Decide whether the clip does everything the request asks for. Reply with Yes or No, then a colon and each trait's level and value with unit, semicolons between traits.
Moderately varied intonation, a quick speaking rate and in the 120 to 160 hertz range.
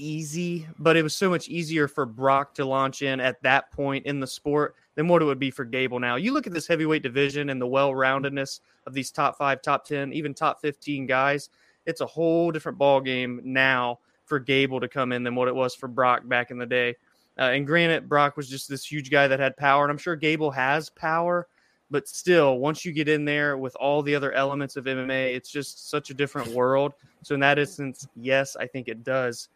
No: narrow, 2.2 semitones; fast, 230 wpm; medium, 140 Hz